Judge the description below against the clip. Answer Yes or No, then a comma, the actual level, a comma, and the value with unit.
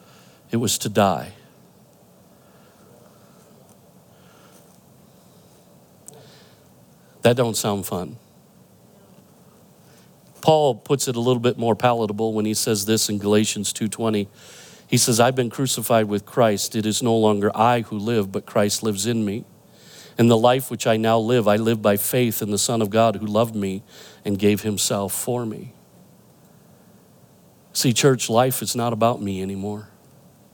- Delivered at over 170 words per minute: No, average, 145 wpm